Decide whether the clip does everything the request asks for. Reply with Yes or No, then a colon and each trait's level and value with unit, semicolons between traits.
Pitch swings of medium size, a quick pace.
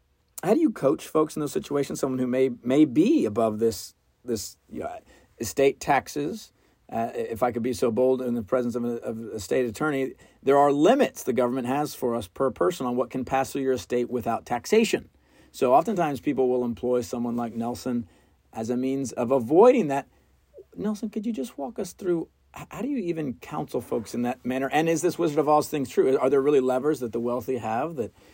Yes: average, 3.5 semitones; fast, 215 wpm